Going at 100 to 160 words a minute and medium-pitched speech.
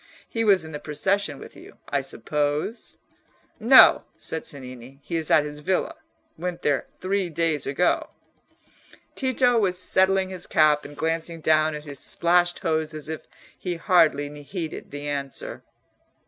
Yes: average, 150 wpm; medium, 160 Hz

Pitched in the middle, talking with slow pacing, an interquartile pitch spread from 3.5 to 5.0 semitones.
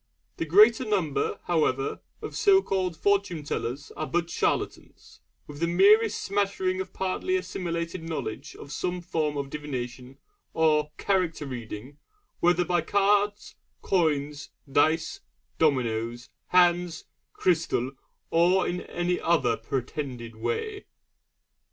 Yes: medium, 165 Hz; slow, 120 wpm; average, 4.5 semitones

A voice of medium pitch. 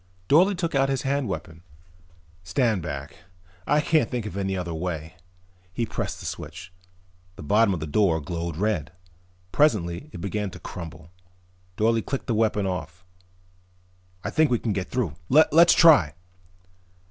No: low, 100 Hz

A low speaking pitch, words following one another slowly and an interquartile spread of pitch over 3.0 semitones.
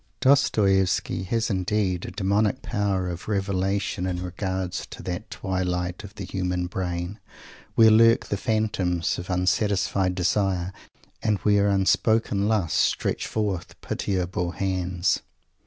No: very low, 95 Hz; slow, 125 wpm; narrow, 2.4 semitones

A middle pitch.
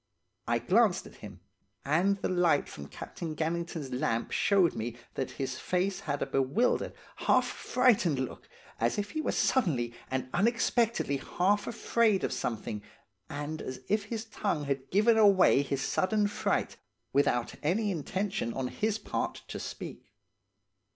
Yes: medium, 175 Hz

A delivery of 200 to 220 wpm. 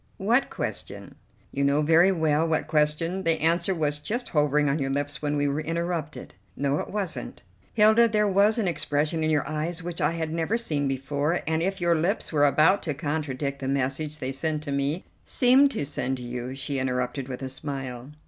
Yes: fast, 205 wpm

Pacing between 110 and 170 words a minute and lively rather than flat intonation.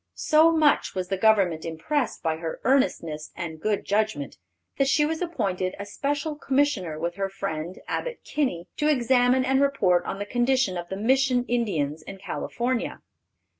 Yes: average, 165 wpm; wide, 7.4 semitones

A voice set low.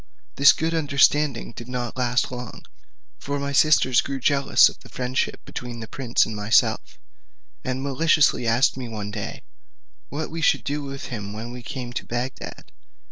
Yes: low, 130 Hz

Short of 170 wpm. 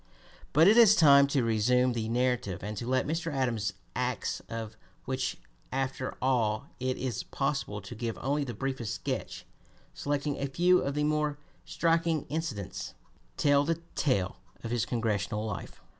Yes: average, 160 wpm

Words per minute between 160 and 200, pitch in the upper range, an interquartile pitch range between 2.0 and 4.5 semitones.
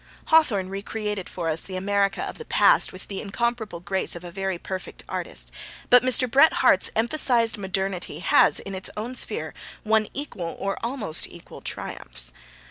Yes: average, 170 wpm; high, 200 Hz; average, 4.1 semitones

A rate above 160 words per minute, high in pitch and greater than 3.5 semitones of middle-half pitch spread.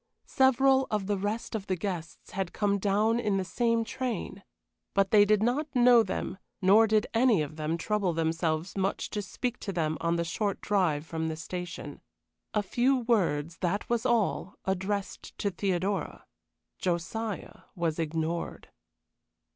No: average, 155 wpm; high, 195 Hz; average, 4.6 semitones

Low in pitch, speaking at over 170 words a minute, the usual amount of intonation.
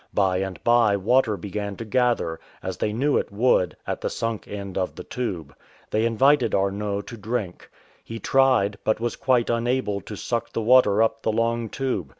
Yes: low, 110 Hz; average, 185 wpm; average, 3.2 semitones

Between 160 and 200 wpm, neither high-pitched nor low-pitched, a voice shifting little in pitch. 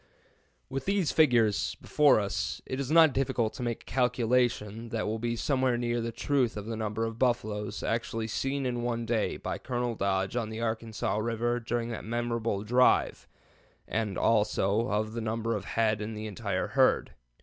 No: average, 180 wpm; low, 115 Hz; narrow, 2.1 semitones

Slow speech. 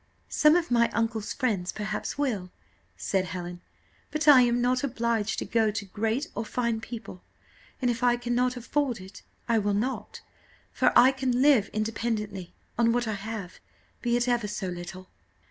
No: average, 170 wpm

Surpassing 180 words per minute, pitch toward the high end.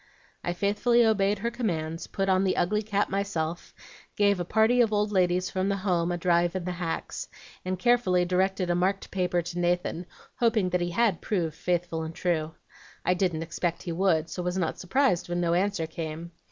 No: average, 195 wpm; medium, 180 Hz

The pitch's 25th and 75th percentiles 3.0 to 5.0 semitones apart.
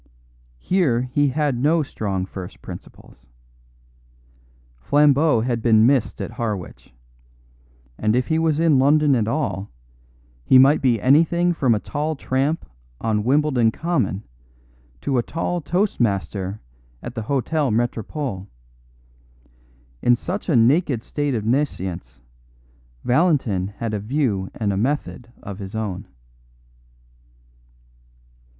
No: wide, 5.6 semitones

